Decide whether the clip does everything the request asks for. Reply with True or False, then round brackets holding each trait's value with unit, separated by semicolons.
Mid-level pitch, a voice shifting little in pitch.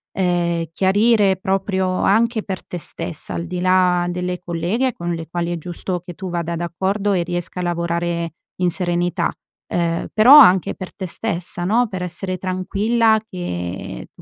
True (180 Hz; 2.0 semitones)